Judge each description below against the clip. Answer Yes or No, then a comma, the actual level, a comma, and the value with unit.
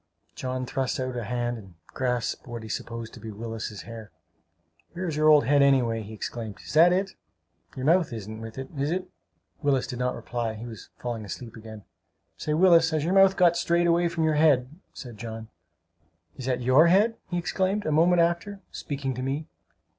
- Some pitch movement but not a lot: No, wide, 6.3 semitones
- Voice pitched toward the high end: No, low, 130 Hz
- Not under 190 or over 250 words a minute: Yes, average, 200 wpm